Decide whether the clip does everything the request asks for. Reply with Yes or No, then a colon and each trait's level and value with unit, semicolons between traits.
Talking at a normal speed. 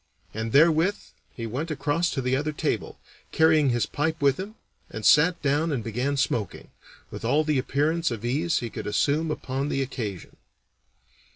Yes: average, 170 wpm